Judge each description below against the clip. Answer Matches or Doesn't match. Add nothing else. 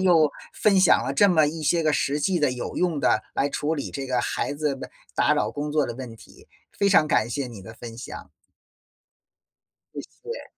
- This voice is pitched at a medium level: Matches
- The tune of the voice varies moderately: Matches